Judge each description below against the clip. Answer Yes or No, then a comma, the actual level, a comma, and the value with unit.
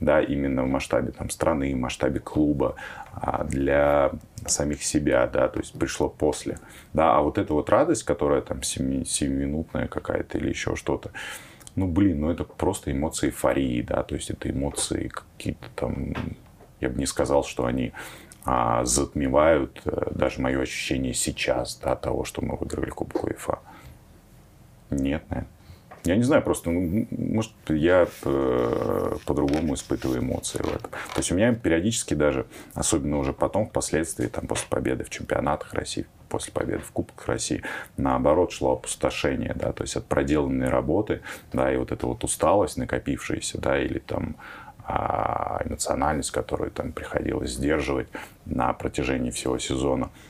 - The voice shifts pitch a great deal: No, average, 2.9 semitones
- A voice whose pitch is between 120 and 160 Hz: No, very low, 70 Hz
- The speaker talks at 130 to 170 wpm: Yes, average, 155 wpm